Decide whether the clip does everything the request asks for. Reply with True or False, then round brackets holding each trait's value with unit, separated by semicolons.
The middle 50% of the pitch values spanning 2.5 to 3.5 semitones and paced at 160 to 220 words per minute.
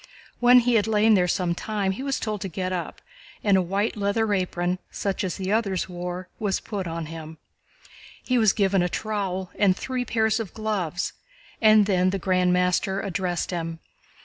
True (3.0 semitones; 185 wpm)